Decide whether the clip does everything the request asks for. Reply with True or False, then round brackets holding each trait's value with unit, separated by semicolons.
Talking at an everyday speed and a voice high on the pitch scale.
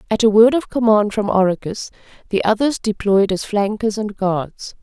True (175 wpm; 210 Hz)